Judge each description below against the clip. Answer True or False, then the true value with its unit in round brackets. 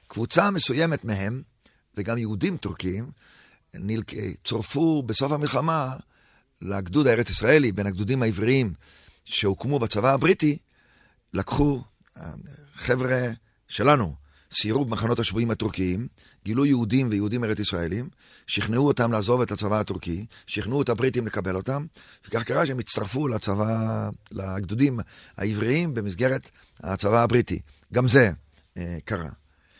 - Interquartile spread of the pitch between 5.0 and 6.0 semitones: False (4.6 semitones)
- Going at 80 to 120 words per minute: True (110 wpm)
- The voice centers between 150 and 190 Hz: False (115 Hz)